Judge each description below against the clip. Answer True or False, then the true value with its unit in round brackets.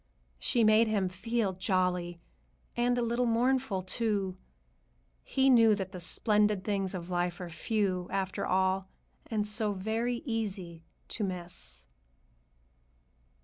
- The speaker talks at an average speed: False (125 wpm)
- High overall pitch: True (200 Hz)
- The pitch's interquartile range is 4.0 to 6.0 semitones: False (3.5 semitones)